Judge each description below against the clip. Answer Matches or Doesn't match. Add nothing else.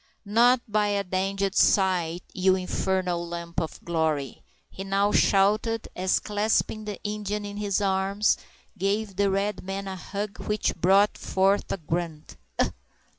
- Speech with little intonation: Matches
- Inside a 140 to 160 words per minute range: Matches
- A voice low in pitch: Doesn't match